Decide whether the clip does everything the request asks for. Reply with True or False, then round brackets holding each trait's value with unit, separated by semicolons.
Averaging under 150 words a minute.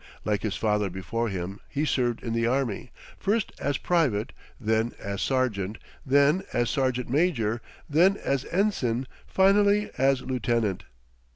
True (135 wpm)